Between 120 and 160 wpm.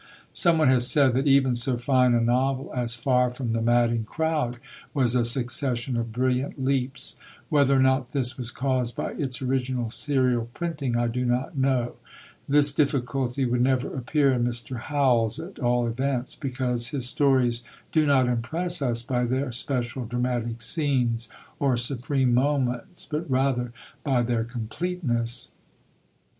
Yes: average, 150 wpm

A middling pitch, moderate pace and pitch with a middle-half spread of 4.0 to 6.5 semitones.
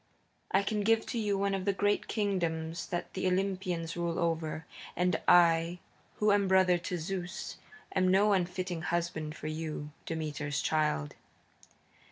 No: medium, 175 Hz; average, 150 wpm; average, 3.1 semitones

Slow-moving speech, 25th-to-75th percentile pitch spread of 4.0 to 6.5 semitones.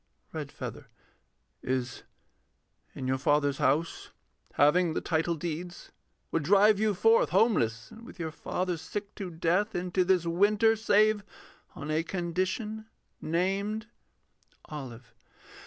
Yes: slow, 120 wpm; average, 5.1 semitones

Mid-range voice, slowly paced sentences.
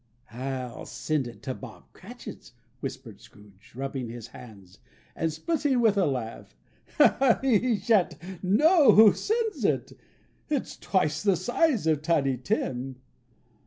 Yes: medium, 160 Hz; slow, 125 wpm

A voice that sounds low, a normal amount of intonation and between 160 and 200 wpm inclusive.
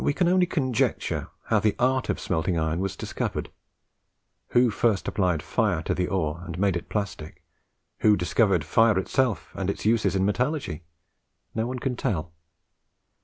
No: low, 100 Hz; wide, 5.7 semitones; average, 165 wpm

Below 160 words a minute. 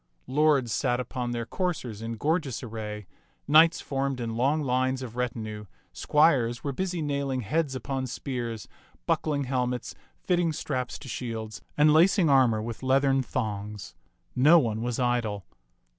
Yes: average, 145 wpm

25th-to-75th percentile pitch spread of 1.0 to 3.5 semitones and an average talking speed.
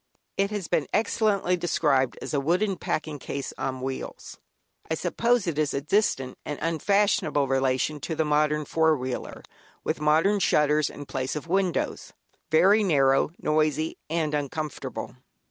No: average, 3.9 semitones; average, 145 wpm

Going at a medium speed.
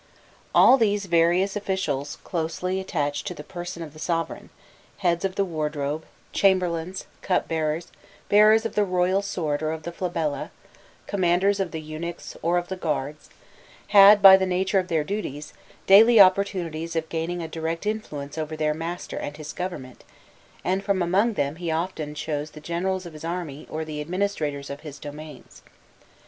Yes: average, 165 wpm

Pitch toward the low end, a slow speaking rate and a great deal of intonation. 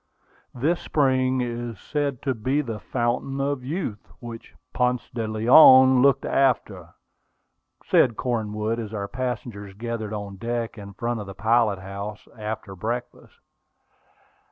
No: low, 115 Hz; slow, 130 wpm; average, 3.3 semitones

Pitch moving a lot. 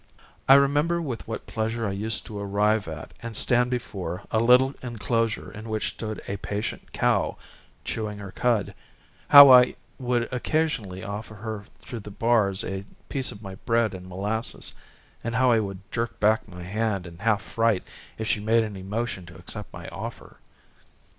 No: average, 2.8 semitones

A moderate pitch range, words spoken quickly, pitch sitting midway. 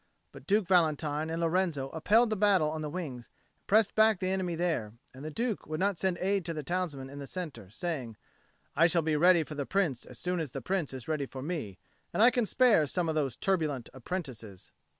Yes: average, 4.8 semitones; fast, 225 wpm; medium, 165 Hz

